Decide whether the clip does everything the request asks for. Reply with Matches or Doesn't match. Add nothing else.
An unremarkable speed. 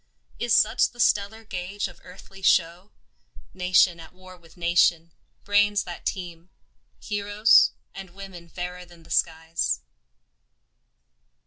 Doesn't match